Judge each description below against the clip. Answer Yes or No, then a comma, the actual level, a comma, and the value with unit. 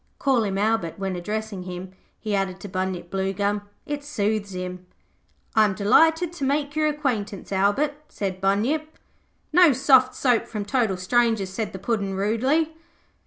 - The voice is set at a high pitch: Yes, high, 210 Hz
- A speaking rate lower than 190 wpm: Yes, average, 155 wpm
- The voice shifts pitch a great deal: Yes, wide, 5.9 semitones